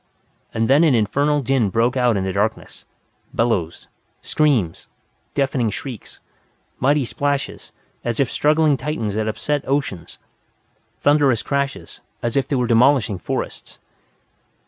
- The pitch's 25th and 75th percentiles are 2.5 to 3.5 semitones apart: No, average, 4.3 semitones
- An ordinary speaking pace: No, slow, 125 wpm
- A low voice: Yes, low, 130 Hz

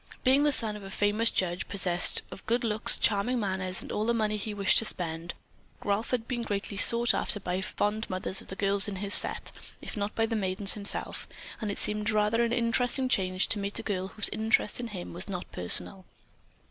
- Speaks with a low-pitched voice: No, high, 205 Hz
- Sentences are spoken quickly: Yes, fast, 220 wpm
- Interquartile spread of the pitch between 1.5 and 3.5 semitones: Yes, average, 2.8 semitones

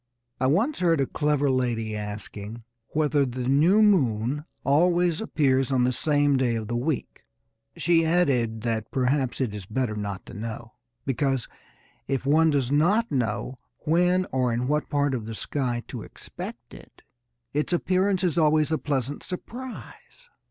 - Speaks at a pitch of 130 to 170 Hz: Yes, medium, 140 Hz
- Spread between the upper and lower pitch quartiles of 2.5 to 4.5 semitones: No, average, 5.1 semitones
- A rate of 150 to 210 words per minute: Yes, average, 160 wpm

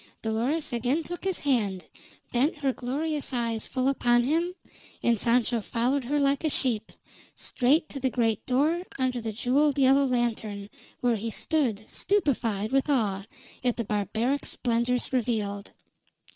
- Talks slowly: No, average, 145 wpm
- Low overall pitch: No, very high, 250 Hz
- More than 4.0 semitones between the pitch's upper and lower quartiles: No, average, 3.7 semitones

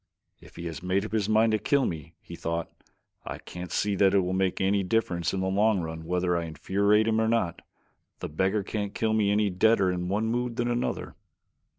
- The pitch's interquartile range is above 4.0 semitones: No, average, 3.6 semitones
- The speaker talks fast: Yes, fast, 220 wpm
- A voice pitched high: No, low, 100 Hz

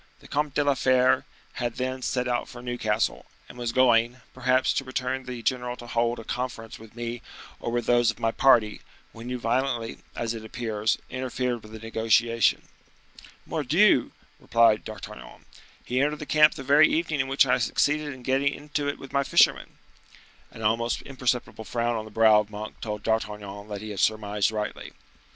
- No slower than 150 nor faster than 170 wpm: No, average, 185 wpm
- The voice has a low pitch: Yes, low, 120 Hz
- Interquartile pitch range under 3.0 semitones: Yes, narrow, 2.6 semitones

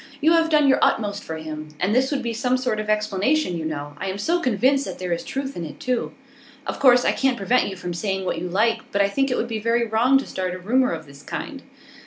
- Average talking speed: No, fast, 270 wpm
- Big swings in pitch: Yes, wide, 5.9 semitones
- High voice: Yes, high, 215 Hz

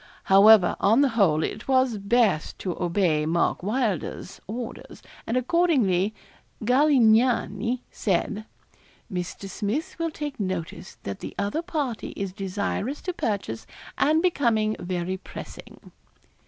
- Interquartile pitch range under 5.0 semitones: No, average, 5.3 semitones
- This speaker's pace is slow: Yes, slow, 120 wpm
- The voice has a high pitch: Yes, high, 215 Hz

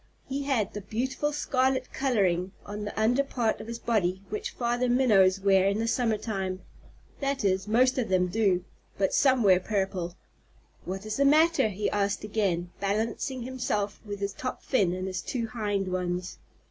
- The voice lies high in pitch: Yes, high, 210 Hz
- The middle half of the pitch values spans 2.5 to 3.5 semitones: No, average, 4.5 semitones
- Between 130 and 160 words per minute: No, average, 175 wpm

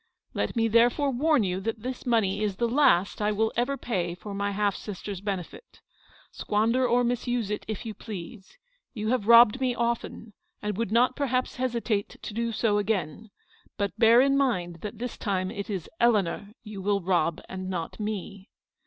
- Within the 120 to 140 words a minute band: No, average, 185 wpm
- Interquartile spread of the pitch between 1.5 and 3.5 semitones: Yes, average, 3.2 semitones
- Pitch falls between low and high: No, high, 215 Hz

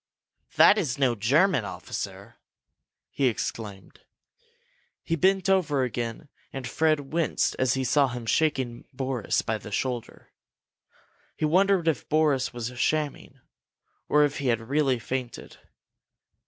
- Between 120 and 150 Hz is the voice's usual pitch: Yes, low, 135 Hz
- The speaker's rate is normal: No, slow, 125 wpm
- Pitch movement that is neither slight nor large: Yes, average, 4.4 semitones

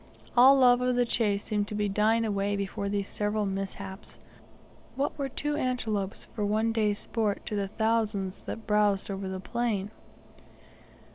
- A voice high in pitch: Yes, high, 210 Hz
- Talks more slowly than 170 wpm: Yes, average, 160 wpm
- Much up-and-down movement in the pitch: No, narrow, 2.4 semitones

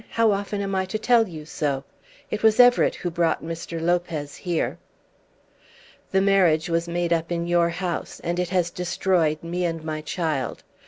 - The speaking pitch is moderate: Yes, medium, 175 Hz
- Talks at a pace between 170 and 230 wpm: Yes, average, 175 wpm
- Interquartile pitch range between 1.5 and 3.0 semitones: Yes, narrow, 2.5 semitones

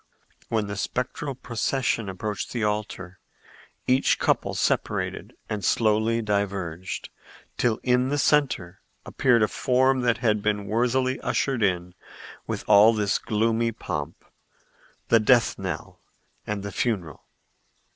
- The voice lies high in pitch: No, low, 110 Hz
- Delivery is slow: Yes, slow, 125 wpm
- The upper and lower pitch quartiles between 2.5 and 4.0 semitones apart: Yes, average, 3.4 semitones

